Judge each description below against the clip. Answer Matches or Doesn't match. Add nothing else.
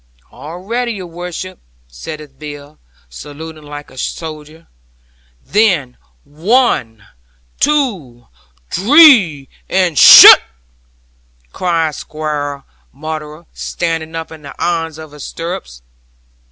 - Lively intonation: Doesn't match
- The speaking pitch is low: Doesn't match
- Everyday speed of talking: Doesn't match